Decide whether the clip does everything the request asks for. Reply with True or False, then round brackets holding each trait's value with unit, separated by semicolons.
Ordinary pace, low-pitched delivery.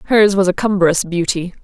False (185 wpm; 185 Hz)